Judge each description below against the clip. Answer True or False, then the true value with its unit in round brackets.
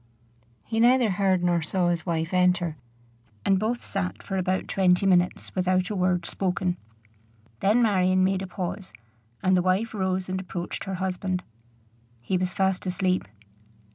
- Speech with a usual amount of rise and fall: False (1.2 semitones)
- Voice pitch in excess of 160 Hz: True (185 Hz)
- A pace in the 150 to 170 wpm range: True (155 wpm)